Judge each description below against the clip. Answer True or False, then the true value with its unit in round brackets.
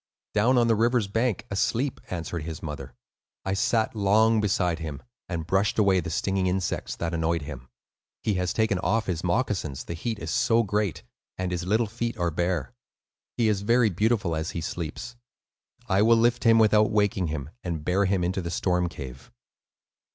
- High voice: False (95 Hz)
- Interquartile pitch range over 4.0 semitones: True (4.6 semitones)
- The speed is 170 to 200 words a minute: True (180 wpm)